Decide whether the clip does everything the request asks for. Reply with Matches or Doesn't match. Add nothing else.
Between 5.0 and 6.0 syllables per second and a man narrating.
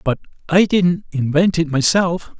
Doesn't match